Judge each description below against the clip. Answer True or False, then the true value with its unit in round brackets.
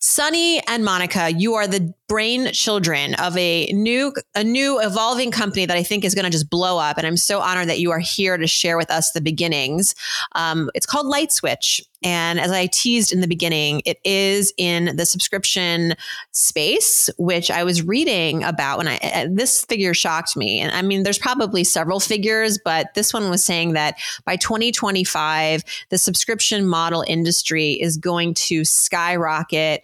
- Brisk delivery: False (180 wpm)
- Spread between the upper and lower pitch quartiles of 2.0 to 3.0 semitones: False (4.1 semitones)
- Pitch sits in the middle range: True (180 Hz)